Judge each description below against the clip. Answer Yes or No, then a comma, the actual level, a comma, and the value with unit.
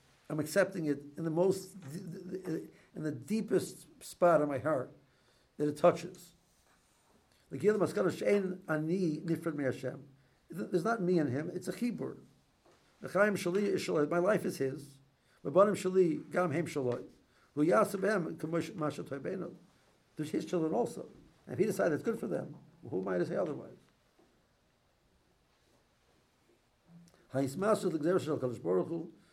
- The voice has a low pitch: No, medium, 165 Hz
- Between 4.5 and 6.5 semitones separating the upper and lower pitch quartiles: No, average, 4.1 semitones